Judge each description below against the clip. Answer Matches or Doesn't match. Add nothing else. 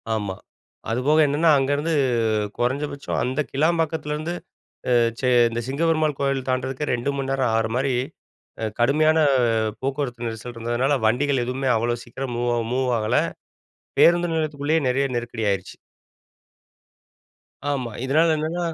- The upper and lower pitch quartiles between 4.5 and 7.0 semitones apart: Doesn't match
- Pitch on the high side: Doesn't match